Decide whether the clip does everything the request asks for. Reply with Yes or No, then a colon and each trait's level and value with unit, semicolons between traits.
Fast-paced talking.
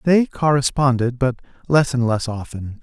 No: average, 150 wpm